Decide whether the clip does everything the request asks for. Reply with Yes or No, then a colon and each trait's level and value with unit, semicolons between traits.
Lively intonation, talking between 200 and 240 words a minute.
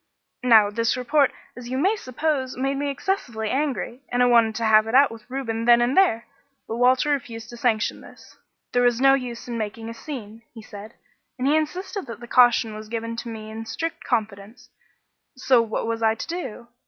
No: average, 3.1 semitones; fast, 205 wpm